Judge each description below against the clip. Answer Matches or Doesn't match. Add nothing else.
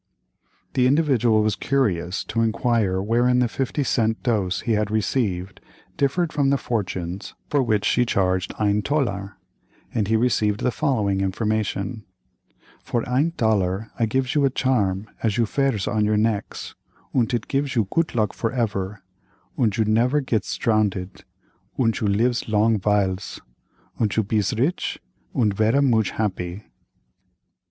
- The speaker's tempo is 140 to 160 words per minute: Matches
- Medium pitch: Doesn't match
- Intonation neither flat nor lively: Matches